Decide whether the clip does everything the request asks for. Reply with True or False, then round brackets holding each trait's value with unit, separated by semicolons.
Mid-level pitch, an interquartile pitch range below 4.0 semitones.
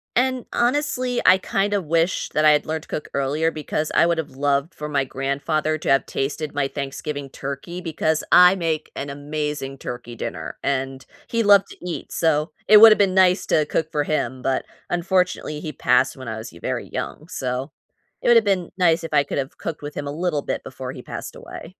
False (155 Hz; 4.4 semitones)